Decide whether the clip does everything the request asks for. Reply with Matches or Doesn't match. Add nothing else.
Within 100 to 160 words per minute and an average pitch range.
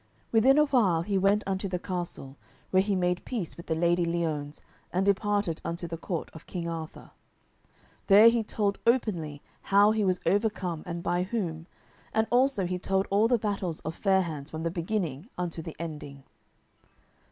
Doesn't match